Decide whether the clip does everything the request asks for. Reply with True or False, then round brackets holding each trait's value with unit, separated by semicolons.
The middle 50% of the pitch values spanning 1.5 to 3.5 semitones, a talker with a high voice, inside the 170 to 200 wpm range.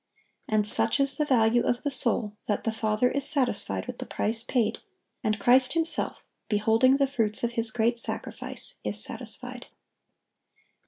False (3.2 semitones; 235 Hz; 160 wpm)